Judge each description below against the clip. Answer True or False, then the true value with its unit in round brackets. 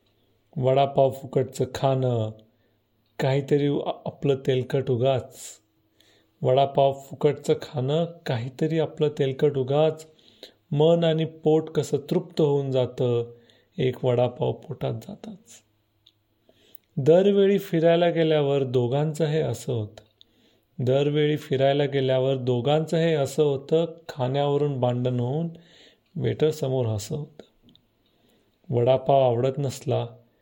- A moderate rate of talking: True (95 wpm)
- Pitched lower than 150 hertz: True (135 Hz)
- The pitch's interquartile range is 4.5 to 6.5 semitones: False (3.8 semitones)